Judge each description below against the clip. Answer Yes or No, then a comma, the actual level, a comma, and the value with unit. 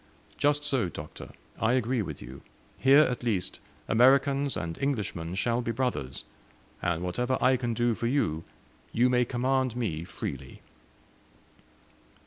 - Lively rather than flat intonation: Yes, wide, 6.6 semitones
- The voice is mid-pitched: No, low, 120 Hz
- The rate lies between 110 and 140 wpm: Yes, slow, 135 wpm